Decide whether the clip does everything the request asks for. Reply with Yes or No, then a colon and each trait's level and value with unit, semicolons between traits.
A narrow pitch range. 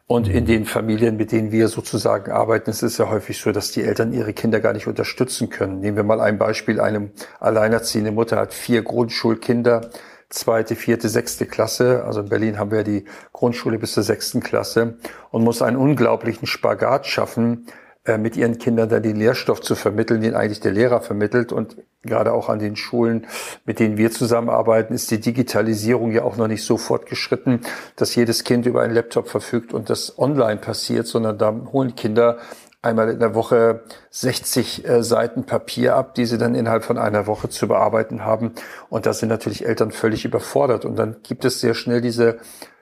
Yes: narrow, 1.3 semitones